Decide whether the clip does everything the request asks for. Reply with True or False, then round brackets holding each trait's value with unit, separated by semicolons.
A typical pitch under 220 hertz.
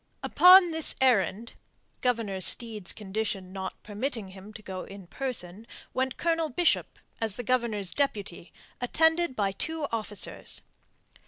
False (225 Hz)